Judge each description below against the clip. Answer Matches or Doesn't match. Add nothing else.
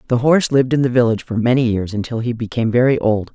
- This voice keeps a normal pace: Doesn't match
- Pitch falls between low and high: Doesn't match